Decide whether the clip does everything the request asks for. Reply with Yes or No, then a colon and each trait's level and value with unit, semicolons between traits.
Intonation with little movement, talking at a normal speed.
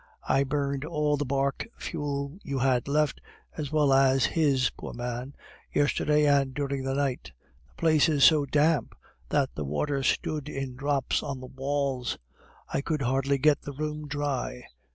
Yes: narrow, 1.8 semitones; average, 165 wpm